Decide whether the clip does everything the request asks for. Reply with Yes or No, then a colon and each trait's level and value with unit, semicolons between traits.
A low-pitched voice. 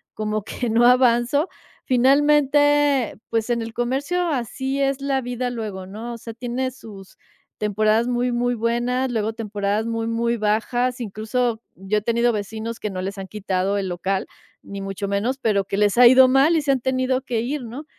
No: high, 235 Hz